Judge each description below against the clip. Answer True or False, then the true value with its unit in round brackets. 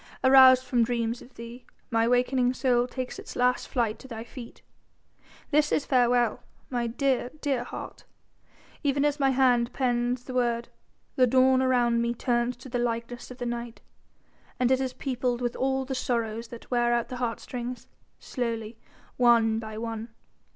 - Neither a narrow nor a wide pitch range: False (1.5 semitones)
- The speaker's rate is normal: True (165 wpm)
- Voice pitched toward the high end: True (245 Hz)